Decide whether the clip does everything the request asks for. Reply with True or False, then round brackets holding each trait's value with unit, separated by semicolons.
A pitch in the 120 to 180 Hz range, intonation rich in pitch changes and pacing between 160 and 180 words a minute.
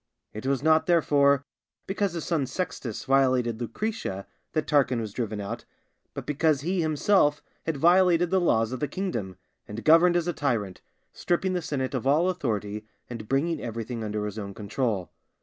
True (135 Hz; 6.9 semitones; 170 wpm)